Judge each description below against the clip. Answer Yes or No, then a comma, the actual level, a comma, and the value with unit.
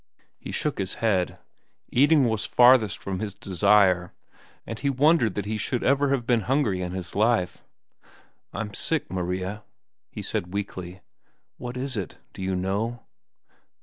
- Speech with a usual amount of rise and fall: Yes, average, 4.7 semitones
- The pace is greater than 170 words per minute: No, average, 150 wpm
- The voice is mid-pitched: No, low, 105 Hz